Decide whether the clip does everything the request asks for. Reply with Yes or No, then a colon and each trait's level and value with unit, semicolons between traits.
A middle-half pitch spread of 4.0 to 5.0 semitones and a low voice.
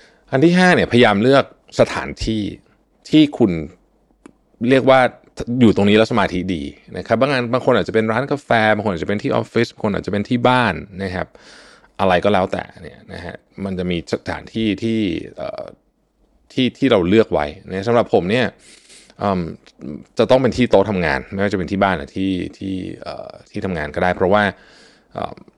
Yes: average, 4.6 semitones; low, 110 Hz